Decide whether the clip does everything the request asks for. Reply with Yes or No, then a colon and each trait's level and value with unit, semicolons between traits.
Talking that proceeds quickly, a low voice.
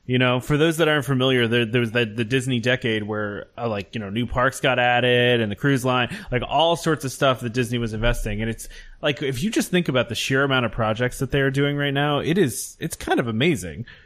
Yes: fast, 265 wpm; low, 125 Hz